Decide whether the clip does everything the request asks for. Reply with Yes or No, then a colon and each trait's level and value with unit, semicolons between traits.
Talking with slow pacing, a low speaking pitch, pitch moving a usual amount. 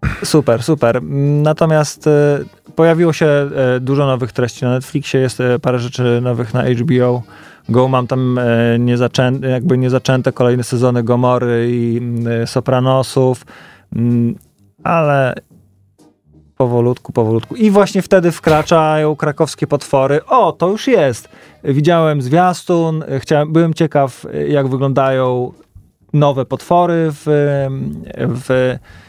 Yes: slow, 105 wpm; low, 130 Hz; average, 3.8 semitones